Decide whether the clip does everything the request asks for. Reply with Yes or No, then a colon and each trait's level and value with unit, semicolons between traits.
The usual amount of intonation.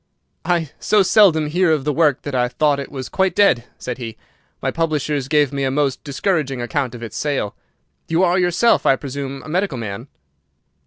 Yes: average, 4.2 semitones